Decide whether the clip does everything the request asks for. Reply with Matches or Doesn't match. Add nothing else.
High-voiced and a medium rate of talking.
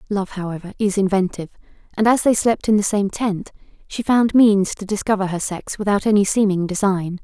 Matches